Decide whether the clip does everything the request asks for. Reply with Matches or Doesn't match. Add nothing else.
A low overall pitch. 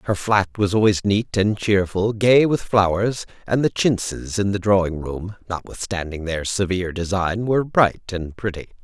Matches